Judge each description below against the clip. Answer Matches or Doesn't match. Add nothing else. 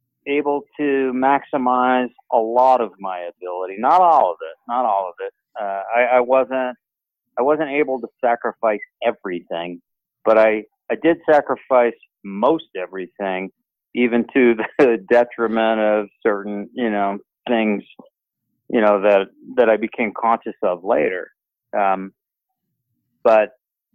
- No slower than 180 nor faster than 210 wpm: Doesn't match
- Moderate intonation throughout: Matches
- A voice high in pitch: Doesn't match